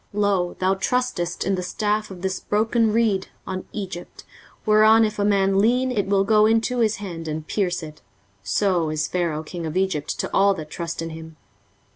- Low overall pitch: No, high, 195 Hz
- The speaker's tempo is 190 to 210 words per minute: Yes, average, 195 wpm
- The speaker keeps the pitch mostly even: No, average, 3.6 semitones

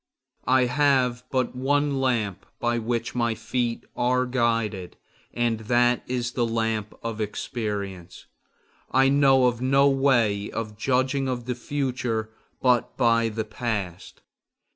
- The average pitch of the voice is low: Yes, low, 120 Hz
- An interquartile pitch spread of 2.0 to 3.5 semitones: Yes, narrow, 2.6 semitones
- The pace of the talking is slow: Yes, slow, 130 wpm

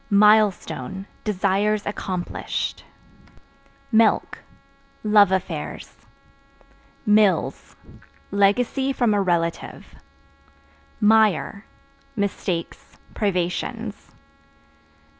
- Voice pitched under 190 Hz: No, high, 205 Hz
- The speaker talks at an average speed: No, slow, 55 wpm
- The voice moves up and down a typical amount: No, narrow, 2.2 semitones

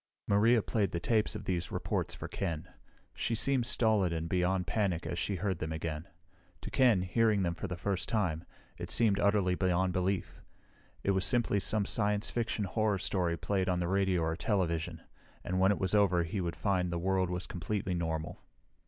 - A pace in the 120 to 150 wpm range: No, average, 190 wpm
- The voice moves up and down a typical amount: Yes, average, 3.0 semitones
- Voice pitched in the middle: No, very low, 95 Hz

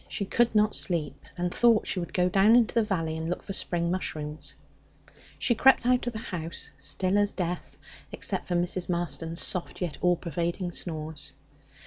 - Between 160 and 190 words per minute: Yes, average, 180 wpm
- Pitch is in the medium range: Yes, medium, 180 Hz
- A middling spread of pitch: Yes, average, 3.7 semitones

